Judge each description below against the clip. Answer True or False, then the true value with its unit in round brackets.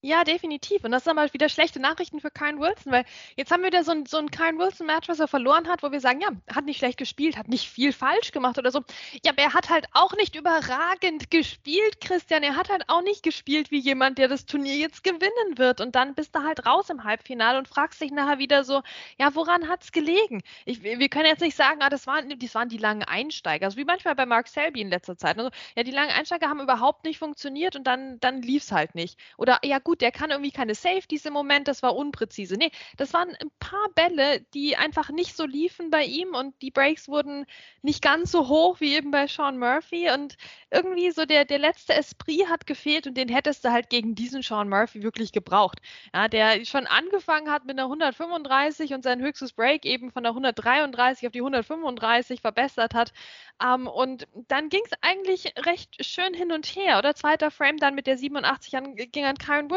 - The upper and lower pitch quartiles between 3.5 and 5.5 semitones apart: True (4.0 semitones)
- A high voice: True (290 Hz)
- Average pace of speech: False (225 wpm)